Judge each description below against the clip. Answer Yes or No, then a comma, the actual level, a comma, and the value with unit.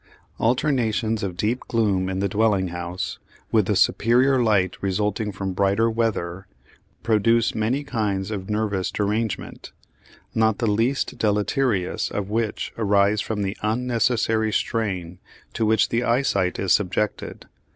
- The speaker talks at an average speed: No, slow, 130 wpm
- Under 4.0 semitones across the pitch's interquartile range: Yes, average, 2.7 semitones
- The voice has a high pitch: No, low, 105 Hz